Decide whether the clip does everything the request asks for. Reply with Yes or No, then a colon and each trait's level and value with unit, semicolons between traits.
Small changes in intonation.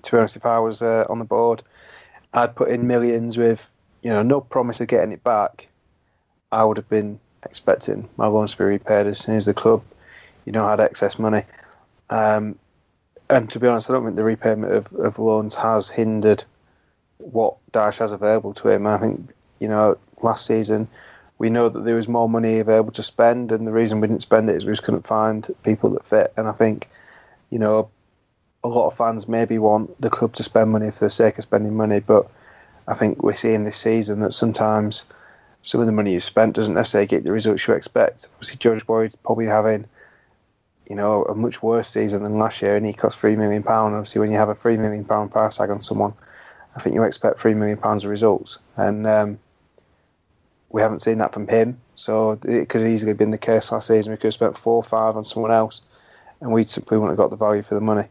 Yes: narrow, 1.0 semitones